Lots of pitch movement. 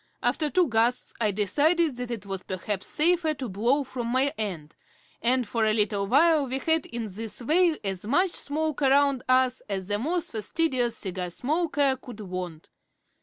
Yes: wide, 6.1 semitones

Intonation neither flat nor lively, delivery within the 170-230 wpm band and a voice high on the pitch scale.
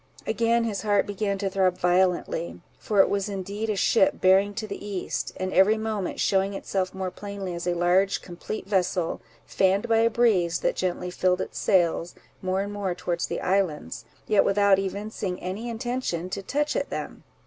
No: narrow, 2.2 semitones; average, 180 wpm; high, 195 Hz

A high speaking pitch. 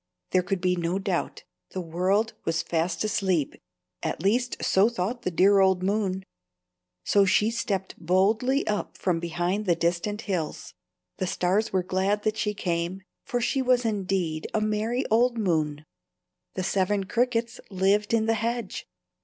Yes: high, 195 Hz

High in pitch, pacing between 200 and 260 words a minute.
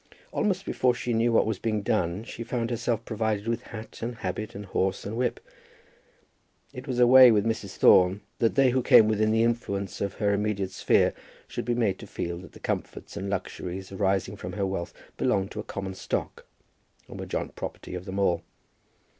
No: low, 105 Hz; fast, 205 wpm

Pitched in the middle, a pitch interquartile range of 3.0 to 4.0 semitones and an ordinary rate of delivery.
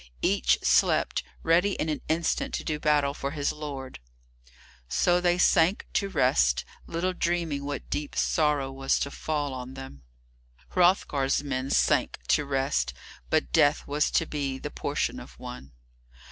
Yes: medium, 145 Hz; average, 3.3 semitones; average, 150 wpm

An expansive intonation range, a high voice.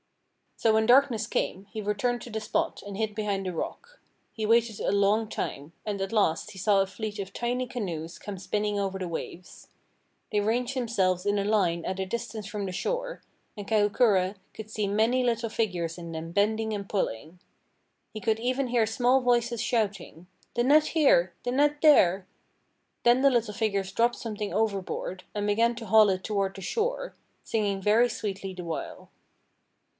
No: average, 3.5 semitones; high, 210 Hz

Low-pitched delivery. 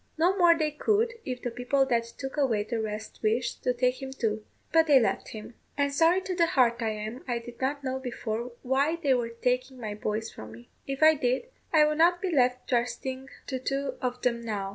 No: very high, 255 Hz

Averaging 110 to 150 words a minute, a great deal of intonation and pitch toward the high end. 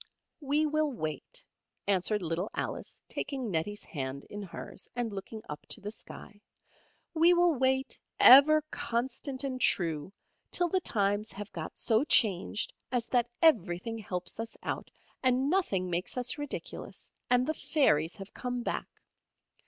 Yes: average, 145 wpm; wide, 6.1 semitones; high, 230 Hz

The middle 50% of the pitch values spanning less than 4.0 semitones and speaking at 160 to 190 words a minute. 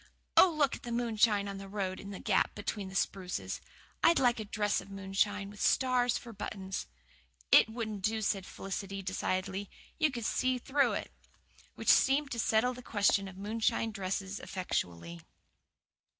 Yes: average, 3.5 semitones; average, 165 wpm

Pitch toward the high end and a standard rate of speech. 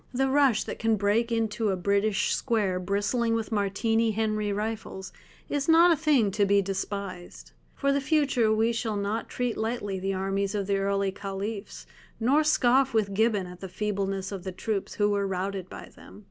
Yes: high, 210 Hz; average, 185 wpm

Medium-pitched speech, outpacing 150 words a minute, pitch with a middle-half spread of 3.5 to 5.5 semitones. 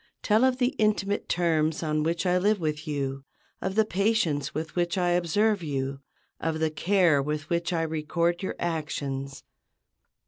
Yes: medium, 165 Hz; average, 165 wpm; average, 3.8 semitones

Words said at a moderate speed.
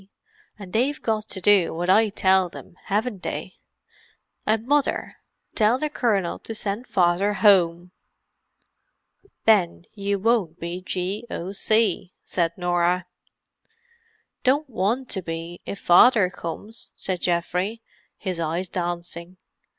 No: slow, 115 wpm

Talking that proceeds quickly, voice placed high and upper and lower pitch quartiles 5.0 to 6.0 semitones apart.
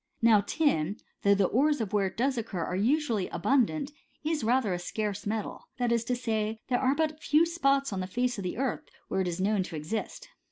Yes: fast, 230 wpm; high, 225 Hz; wide, 5.4 semitones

